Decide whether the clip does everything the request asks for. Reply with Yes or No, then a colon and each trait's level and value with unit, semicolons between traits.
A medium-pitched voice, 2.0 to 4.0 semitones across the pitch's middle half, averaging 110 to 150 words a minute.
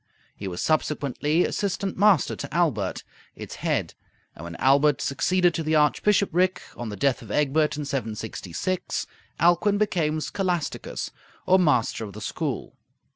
No: medium, 150 Hz; average, 5.2 semitones; average, 140 wpm